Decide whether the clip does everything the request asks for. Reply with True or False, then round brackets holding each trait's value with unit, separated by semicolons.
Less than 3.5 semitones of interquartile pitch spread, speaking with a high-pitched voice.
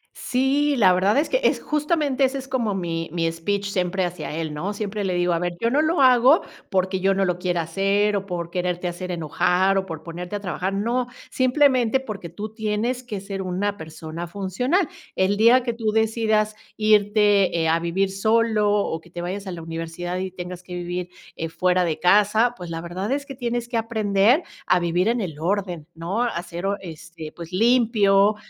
False (4.3 semitones; 195 Hz)